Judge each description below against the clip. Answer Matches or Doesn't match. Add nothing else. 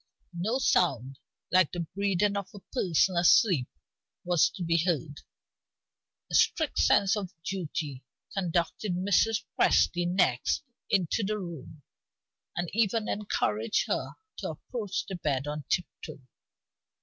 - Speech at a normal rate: Doesn't match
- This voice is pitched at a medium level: Matches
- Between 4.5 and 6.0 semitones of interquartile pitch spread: Doesn't match